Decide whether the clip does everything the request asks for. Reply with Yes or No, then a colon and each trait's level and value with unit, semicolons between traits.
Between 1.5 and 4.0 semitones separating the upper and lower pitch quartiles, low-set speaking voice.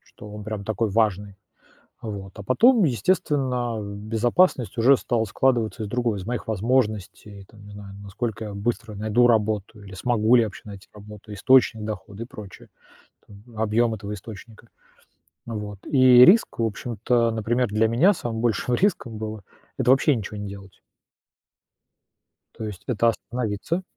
Yes: average, 2.8 semitones; low, 110 Hz